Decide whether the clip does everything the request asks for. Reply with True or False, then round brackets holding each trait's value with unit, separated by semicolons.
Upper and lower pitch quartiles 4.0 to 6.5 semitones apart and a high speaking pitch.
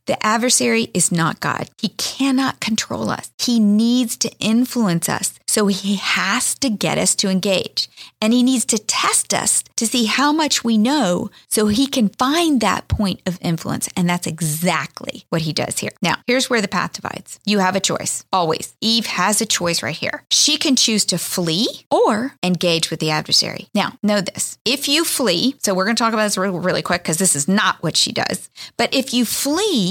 True (5.0 semitones; 215 Hz)